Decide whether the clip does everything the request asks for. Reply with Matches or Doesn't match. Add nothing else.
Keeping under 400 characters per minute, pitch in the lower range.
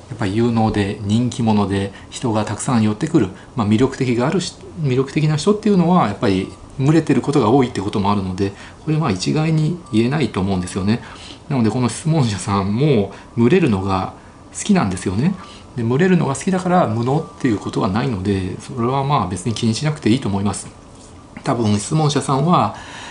Doesn't match